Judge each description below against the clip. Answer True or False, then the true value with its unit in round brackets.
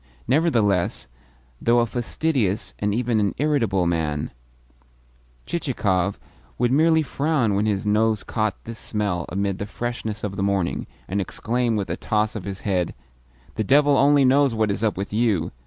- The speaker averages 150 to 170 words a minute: True (160 wpm)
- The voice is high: False (110 Hz)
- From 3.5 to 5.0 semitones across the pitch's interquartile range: True (3.9 semitones)